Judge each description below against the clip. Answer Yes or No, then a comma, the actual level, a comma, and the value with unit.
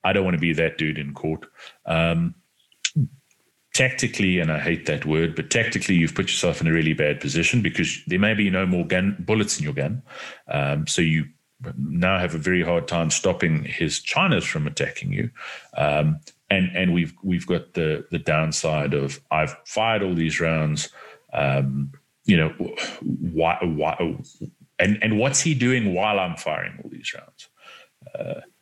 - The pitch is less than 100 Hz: Yes, very low, 85 Hz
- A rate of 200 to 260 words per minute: No, average, 175 wpm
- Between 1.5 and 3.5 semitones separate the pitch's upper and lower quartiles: No, average, 4.4 semitones